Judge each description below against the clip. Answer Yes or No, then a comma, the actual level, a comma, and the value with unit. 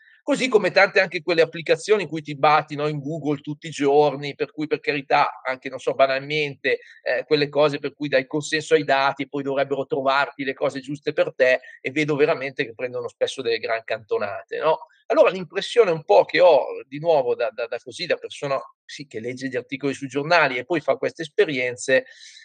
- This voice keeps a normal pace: No, fast, 210 wpm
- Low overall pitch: No, medium, 150 Hz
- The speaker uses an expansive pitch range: Yes, wide, 7.3 semitones